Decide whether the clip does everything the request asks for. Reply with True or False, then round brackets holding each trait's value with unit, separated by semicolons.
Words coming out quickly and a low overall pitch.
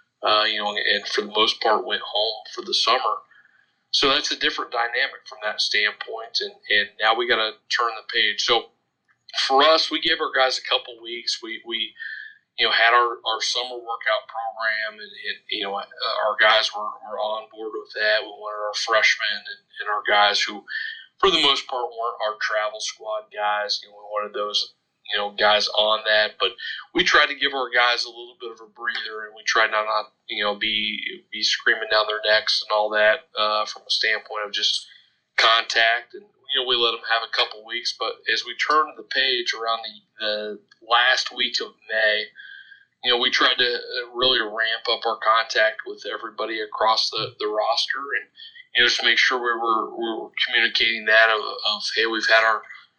True (210 wpm; 115 Hz)